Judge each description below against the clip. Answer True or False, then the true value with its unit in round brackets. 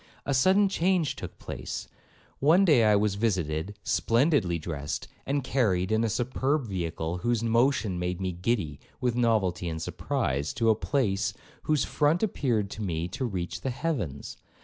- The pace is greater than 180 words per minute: False (155 wpm)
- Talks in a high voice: False (110 Hz)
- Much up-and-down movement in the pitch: True (7.0 semitones)